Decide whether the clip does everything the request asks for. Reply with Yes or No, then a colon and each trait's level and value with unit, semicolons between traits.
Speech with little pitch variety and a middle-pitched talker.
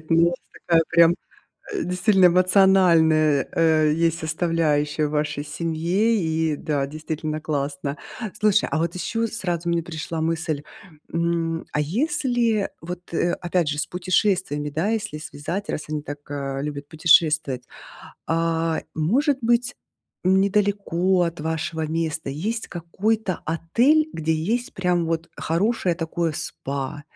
No: average, 3.1 semitones; medium, 165 Hz